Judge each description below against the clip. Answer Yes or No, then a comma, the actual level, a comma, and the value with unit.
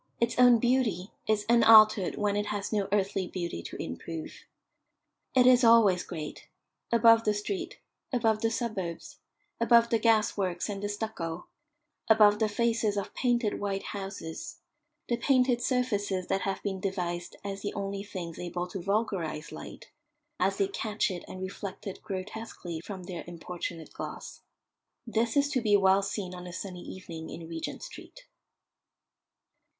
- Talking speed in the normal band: Yes, average, 155 wpm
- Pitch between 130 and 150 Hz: No, high, 200 Hz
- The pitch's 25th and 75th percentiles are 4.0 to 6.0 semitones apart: No, average, 3.6 semitones